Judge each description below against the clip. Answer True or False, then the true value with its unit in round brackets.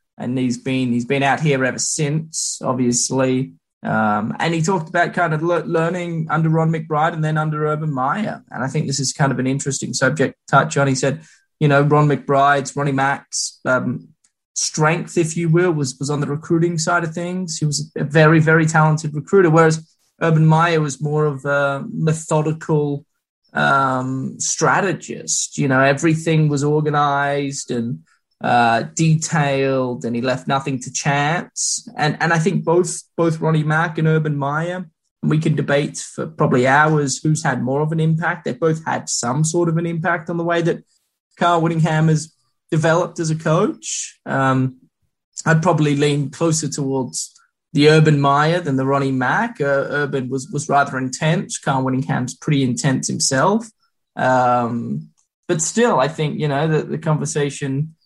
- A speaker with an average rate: True (175 wpm)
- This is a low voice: False (150 Hz)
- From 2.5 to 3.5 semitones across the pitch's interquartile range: True (3.0 semitones)